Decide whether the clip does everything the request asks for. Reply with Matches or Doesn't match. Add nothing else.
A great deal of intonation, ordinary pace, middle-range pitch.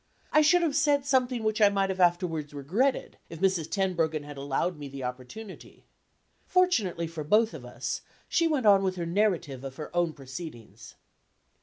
Matches